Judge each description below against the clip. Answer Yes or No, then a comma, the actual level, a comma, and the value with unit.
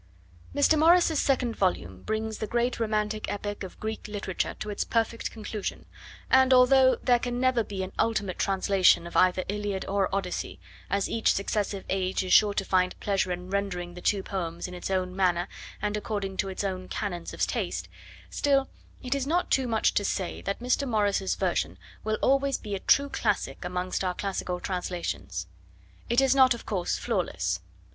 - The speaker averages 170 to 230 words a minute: Yes, average, 180 wpm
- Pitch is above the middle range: Yes, high, 200 Hz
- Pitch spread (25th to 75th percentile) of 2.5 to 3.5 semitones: No, average, 4.2 semitones